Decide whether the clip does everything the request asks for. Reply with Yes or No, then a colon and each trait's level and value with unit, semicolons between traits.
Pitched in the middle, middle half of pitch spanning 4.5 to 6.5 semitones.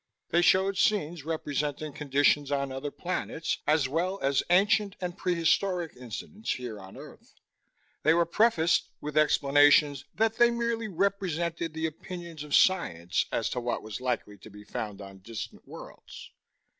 Yes: medium, 155 Hz; average, 5.1 semitones